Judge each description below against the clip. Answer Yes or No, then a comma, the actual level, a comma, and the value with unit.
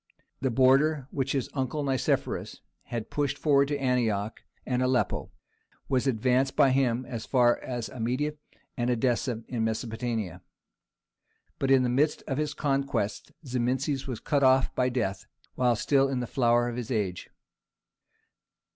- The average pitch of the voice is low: Yes, low, 125 Hz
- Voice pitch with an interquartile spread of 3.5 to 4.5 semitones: No, narrow, 2.4 semitones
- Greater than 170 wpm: No, average, 145 wpm